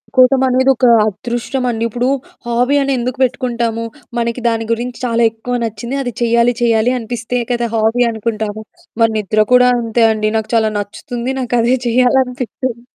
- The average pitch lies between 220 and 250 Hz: Yes, high, 235 Hz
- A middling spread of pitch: No, narrow, 1.7 semitones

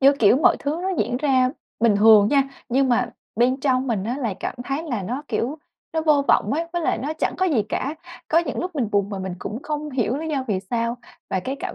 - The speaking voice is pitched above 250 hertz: Yes, very high, 260 Hz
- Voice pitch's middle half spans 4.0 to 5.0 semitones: Yes, average, 4.7 semitones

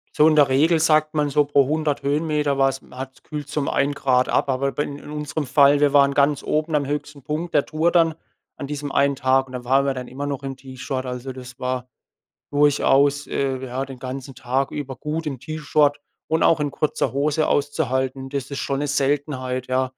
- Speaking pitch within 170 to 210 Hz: No, medium, 140 Hz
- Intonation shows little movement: Yes, narrow, 2.0 semitones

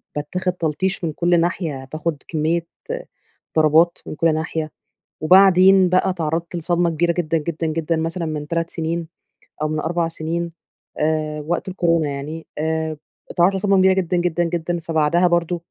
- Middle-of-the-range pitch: Yes, medium, 165 Hz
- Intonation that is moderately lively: No, narrow, 1.8 semitones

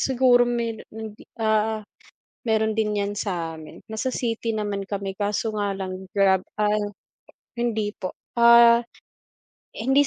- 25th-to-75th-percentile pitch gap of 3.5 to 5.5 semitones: No, narrow, 2.6 semitones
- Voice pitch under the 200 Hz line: No, high, 215 Hz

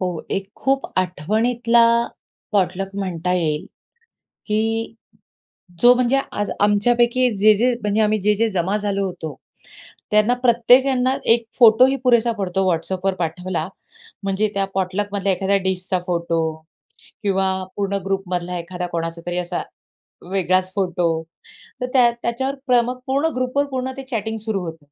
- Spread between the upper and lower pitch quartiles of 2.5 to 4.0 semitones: No, average, 4.6 semitones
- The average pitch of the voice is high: Yes, high, 200 Hz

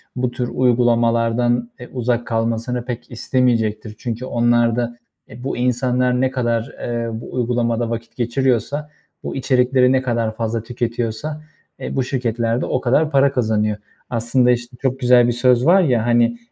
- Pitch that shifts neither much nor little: No, narrow, 1.4 semitones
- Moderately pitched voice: No, low, 120 Hz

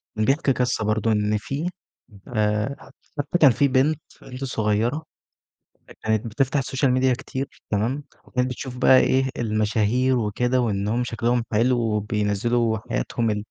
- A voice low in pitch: Yes, low, 120 Hz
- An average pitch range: Yes, average, 3.5 semitones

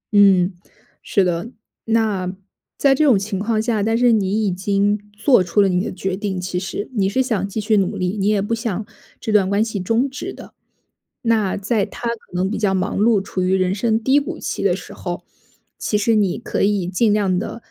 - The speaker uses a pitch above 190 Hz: Yes, high, 205 Hz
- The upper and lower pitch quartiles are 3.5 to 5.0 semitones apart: No, average, 2.8 semitones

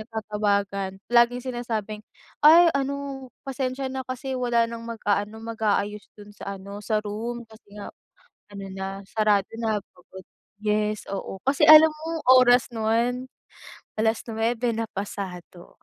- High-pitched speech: Yes, high, 225 Hz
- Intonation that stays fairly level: No, average, 3.4 semitones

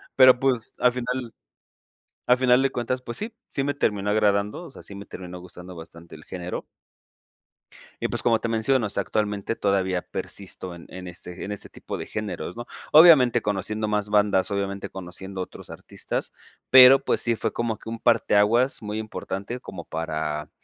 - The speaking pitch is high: No, low, 105 Hz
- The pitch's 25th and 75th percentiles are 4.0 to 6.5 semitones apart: Yes, average, 4.4 semitones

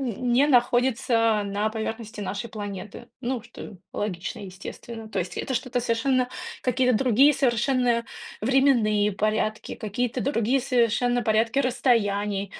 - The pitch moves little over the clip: No, average, 3.0 semitones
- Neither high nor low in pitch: No, high, 235 Hz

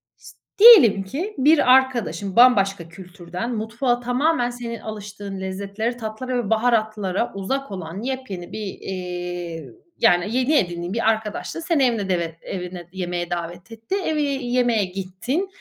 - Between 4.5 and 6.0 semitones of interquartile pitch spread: Yes, average, 5.2 semitones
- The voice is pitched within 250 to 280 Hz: No, high, 215 Hz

